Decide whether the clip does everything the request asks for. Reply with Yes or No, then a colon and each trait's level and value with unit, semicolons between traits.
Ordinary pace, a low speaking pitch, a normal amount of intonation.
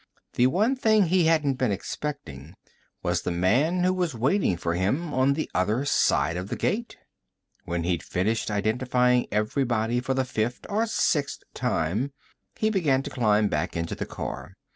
No: average, 165 wpm; low, 125 Hz; wide, 8.2 semitones